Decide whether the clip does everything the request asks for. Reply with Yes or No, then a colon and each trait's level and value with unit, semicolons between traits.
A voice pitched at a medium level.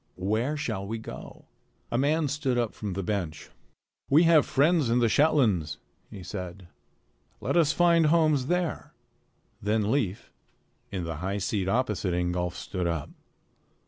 No: low, 110 Hz